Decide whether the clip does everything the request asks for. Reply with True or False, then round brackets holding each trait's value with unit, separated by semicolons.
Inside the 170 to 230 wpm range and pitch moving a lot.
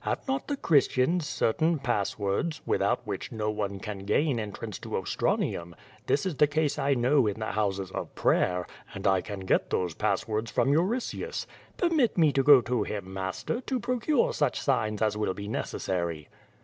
True (175 wpm; 7.7 semitones)